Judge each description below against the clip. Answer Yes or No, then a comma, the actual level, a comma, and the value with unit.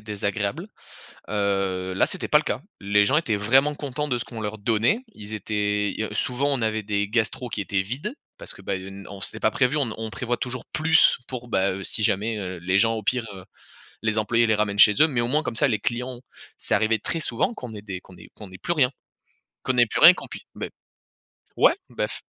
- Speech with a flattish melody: No, average, 3.6 semitones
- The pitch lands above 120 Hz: No, low, 110 Hz